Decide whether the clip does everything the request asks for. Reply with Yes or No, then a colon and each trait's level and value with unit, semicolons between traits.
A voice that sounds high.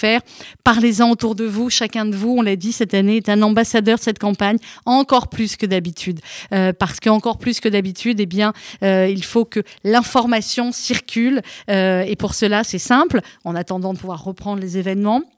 Yes: high, 215 Hz